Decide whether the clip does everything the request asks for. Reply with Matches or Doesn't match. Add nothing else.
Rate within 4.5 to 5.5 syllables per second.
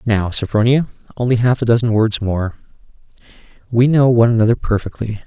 Doesn't match